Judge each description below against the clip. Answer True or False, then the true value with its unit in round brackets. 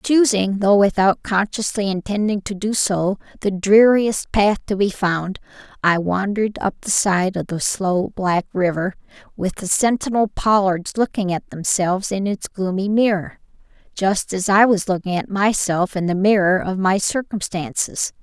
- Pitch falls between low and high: False (195 Hz)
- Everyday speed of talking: True (160 wpm)